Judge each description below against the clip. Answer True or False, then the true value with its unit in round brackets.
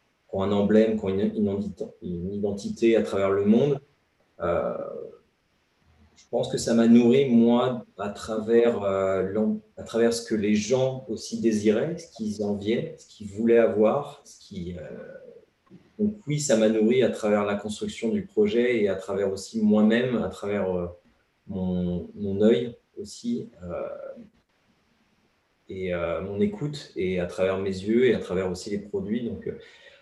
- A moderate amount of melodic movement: False (6.2 semitones)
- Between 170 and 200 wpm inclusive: False (160 wpm)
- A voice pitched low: True (110 Hz)